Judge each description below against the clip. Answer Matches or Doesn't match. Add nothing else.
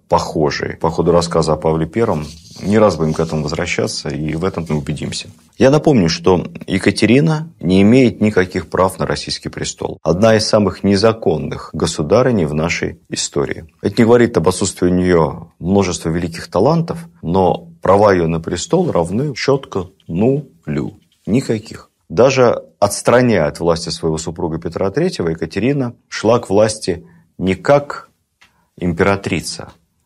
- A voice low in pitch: Matches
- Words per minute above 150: Doesn't match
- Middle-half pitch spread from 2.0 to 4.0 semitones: Doesn't match